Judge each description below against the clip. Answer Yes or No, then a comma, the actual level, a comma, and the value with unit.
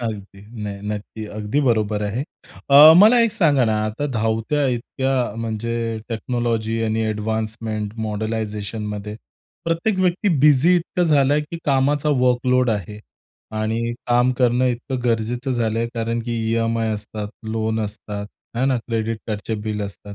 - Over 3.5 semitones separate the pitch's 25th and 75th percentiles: No, average, 3.1 semitones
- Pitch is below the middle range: Yes, low, 115 Hz